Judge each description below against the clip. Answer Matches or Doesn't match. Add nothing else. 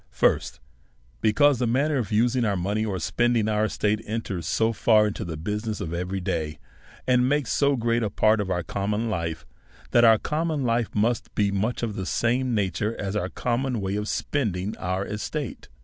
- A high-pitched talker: Doesn't match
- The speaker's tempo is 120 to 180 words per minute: Doesn't match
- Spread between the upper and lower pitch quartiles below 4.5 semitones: Matches